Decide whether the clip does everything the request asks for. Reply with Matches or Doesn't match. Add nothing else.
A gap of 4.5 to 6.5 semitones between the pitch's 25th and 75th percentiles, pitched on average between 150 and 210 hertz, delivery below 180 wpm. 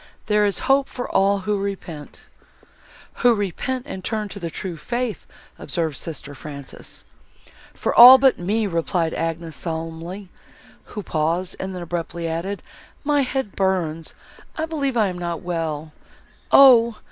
Matches